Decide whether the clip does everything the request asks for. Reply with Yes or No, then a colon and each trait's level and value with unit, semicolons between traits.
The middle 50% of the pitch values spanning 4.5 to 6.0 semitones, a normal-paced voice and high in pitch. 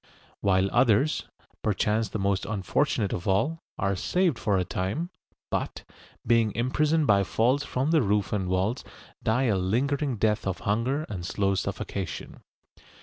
No: average, 5.3 semitones; average, 145 wpm; low, 110 Hz